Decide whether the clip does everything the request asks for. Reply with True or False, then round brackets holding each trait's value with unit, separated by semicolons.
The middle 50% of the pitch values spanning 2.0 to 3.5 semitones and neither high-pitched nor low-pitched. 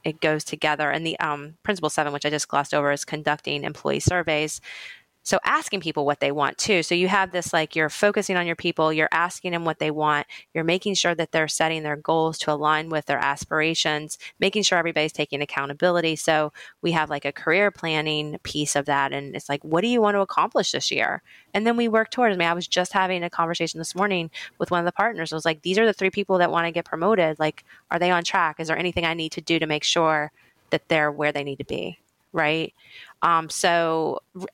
True (2.6 semitones; 160 Hz)